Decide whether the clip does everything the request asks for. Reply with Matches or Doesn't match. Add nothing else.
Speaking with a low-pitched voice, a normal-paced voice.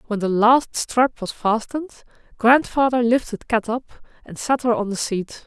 Doesn't match